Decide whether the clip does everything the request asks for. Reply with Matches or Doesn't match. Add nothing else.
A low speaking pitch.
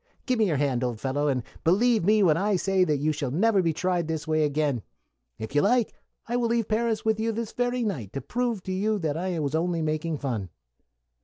Doesn't match